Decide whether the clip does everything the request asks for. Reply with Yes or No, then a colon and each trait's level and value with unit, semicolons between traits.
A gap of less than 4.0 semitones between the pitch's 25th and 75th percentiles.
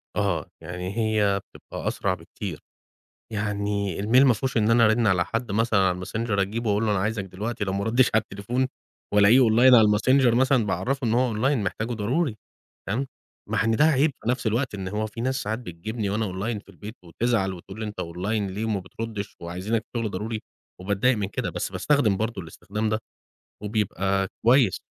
Yes: average, 2.9 semitones